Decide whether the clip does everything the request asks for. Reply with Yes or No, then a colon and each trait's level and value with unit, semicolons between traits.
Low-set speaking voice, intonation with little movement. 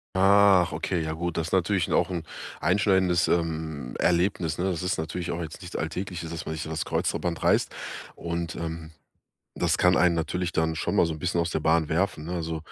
Yes: very low, 85 Hz; narrow, 2.0 semitones